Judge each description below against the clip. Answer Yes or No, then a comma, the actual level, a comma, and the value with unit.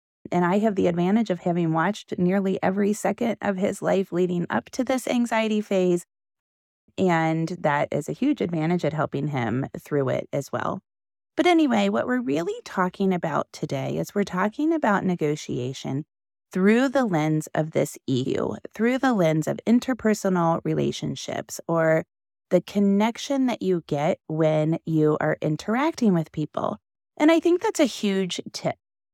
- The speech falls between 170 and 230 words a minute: No, average, 160 wpm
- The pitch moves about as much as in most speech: No, wide, 5.7 semitones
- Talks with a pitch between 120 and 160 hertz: No, medium, 185 Hz